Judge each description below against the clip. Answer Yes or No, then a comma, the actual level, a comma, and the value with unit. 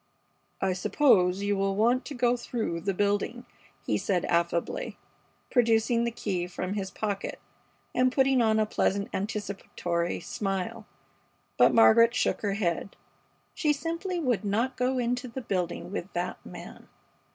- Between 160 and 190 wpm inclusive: No, average, 145 wpm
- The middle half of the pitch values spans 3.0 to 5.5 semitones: Yes, average, 4.1 semitones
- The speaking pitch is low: No, high, 215 Hz